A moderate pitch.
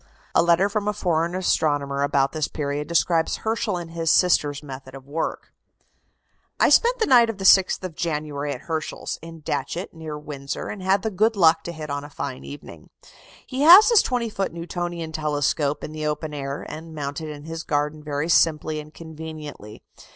Yes: medium, 160 Hz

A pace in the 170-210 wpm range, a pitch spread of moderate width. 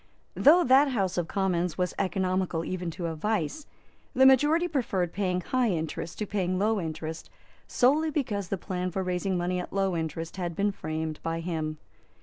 Yes: average, 175 wpm; average, 4.0 semitones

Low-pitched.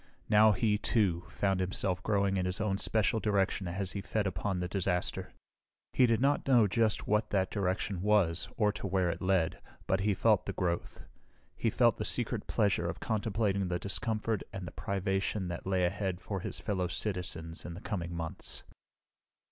Yes: very low, 95 Hz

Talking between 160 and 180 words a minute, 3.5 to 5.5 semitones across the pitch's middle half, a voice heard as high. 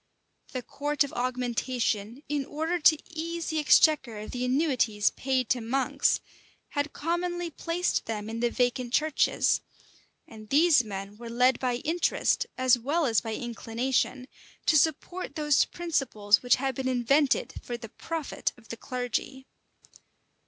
No: average, 145 wpm; average, 4.2 semitones; very high, 255 Hz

